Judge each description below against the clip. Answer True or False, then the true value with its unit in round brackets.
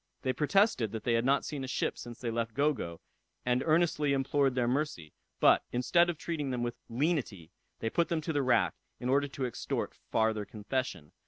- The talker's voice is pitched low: True (130 Hz)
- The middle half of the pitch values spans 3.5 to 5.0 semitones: True (4.3 semitones)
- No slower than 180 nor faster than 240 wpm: True (195 wpm)